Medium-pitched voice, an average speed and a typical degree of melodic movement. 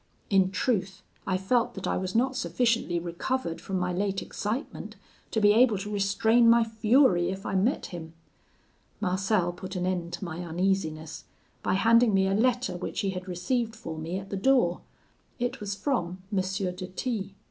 No: high, 195 Hz; average, 180 wpm; average, 3.8 semitones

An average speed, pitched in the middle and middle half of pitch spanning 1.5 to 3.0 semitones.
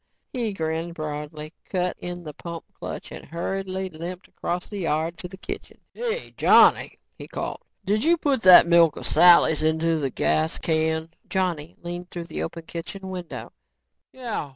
Yes: average, 160 wpm; medium, 170 Hz; average, 2.7 semitones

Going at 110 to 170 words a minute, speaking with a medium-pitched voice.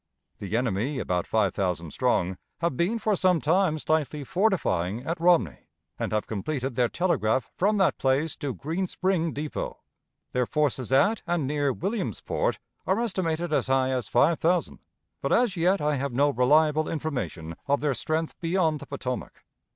Yes: average, 165 wpm; medium, 150 Hz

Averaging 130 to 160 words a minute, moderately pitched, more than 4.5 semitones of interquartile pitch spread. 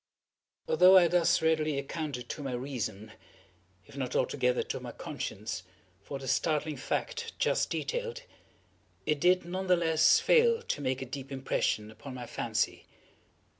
Yes: average, 150 wpm; medium, 145 Hz; average, 5.2 semitones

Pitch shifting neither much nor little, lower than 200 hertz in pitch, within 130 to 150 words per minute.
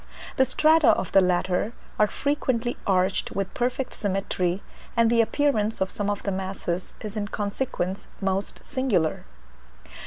No: average, 4.1 semitones; high, 205 Hz; average, 145 wpm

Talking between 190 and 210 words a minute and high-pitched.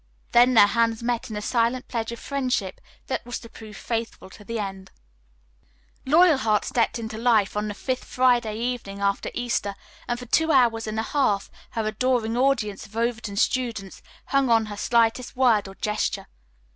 No: average, 175 wpm; high, 230 Hz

